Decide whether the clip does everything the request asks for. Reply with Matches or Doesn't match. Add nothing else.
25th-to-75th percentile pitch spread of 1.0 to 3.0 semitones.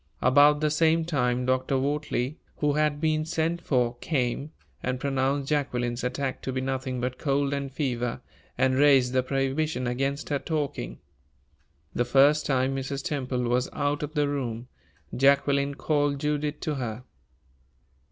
Matches